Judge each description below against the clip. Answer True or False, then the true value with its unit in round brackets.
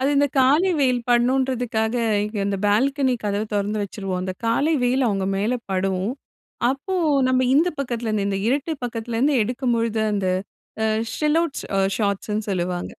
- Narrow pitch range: False (4.4 semitones)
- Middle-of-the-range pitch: False (230 Hz)